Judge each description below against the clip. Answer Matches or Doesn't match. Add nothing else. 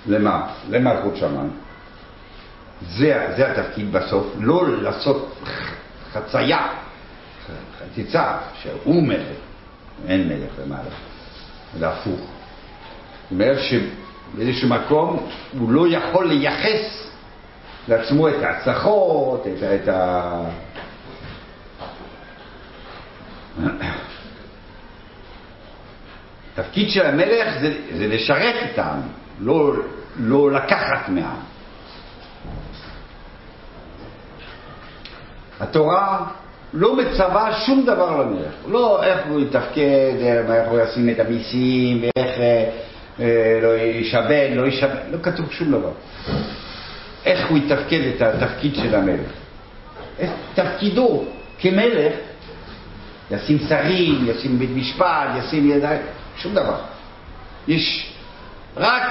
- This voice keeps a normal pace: Doesn't match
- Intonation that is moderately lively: Doesn't match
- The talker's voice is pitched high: Doesn't match